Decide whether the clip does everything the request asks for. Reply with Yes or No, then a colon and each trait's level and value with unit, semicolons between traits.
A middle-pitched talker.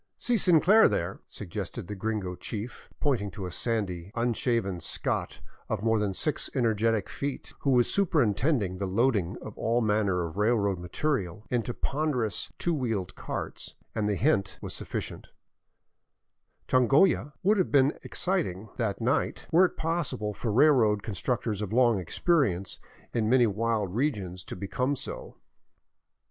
No: low, 115 Hz